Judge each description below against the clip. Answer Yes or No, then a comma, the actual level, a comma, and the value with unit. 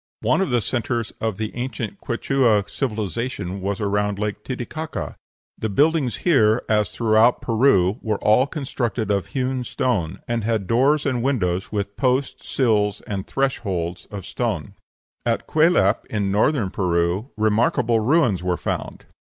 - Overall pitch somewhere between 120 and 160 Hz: No, low, 110 Hz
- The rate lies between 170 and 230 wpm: No, average, 145 wpm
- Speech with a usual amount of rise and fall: Yes, average, 4.1 semitones